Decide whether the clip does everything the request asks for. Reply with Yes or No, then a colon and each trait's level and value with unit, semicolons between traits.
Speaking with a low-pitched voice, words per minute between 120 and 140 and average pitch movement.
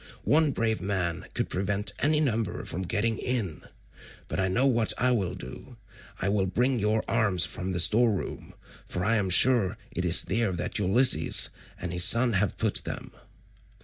No: low, 100 Hz; average, 180 wpm; average, 4.2 semitones